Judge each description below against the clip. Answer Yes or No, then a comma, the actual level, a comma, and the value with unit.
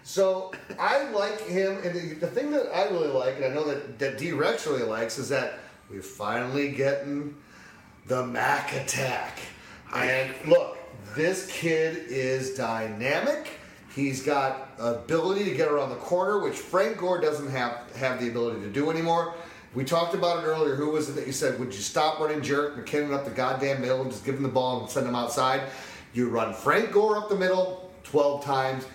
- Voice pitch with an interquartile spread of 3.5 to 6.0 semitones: Yes, average, 5.1 semitones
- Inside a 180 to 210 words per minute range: Yes, average, 195 wpm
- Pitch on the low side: No, medium, 145 Hz